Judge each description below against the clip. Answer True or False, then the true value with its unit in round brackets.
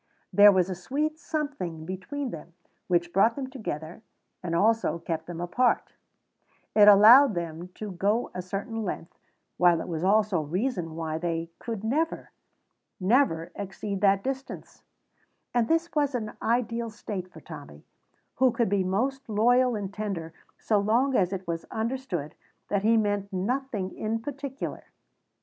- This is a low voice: False (205 Hz)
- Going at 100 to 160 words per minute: True (155 wpm)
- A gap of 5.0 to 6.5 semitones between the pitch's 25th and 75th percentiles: True (5.5 semitones)